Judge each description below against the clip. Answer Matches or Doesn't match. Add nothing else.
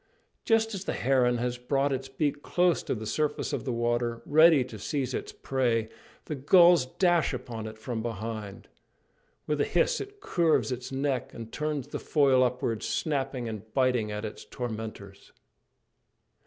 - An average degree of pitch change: Matches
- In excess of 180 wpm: Doesn't match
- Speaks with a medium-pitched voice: Doesn't match